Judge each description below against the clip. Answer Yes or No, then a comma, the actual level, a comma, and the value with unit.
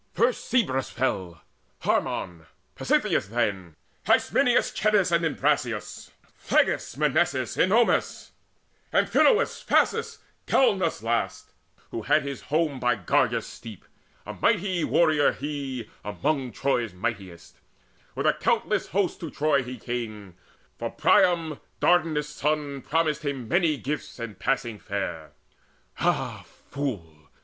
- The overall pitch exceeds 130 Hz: Yes, medium, 140 Hz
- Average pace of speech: No, slow, 115 wpm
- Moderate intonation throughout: No, wide, 6.0 semitones